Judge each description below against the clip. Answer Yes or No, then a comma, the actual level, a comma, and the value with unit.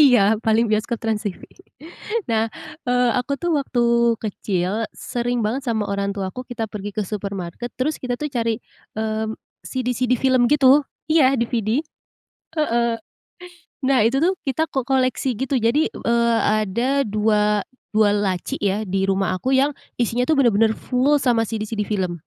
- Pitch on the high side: Yes, high, 235 Hz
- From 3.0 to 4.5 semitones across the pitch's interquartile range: Yes, average, 3.6 semitones